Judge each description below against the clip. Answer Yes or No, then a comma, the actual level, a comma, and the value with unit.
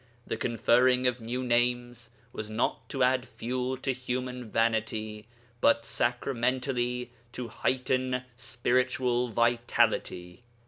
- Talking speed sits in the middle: No, slow, 105 wpm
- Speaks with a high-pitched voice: No, low, 120 Hz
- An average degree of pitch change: No, narrow, 1.6 semitones